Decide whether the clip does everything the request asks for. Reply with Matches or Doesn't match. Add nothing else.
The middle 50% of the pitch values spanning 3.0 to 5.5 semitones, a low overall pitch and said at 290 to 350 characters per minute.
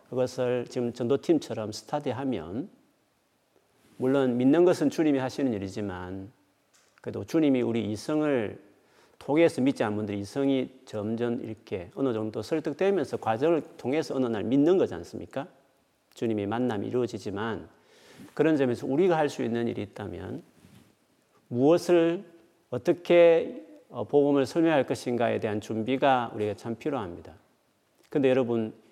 Matches